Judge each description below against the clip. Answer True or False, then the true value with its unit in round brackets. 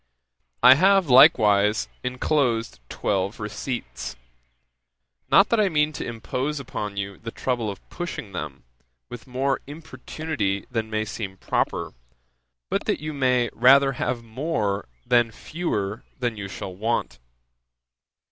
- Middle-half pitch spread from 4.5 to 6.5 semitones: True (5.2 semitones)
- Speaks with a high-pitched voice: False (120 Hz)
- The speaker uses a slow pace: True (130 wpm)